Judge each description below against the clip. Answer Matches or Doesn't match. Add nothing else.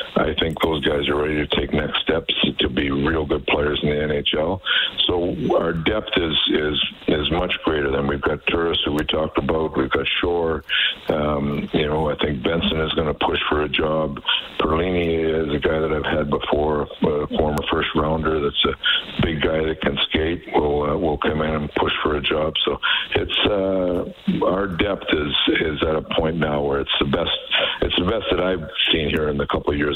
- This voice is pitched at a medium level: Doesn't match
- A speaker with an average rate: Doesn't match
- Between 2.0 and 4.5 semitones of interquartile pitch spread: Doesn't match